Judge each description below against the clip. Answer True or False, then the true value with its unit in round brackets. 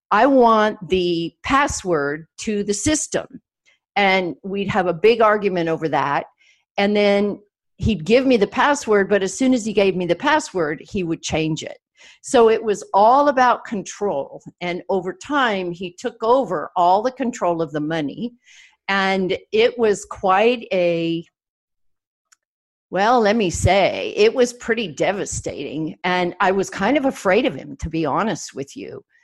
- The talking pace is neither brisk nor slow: True (160 wpm)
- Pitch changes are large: True (5.7 semitones)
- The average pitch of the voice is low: False (200 Hz)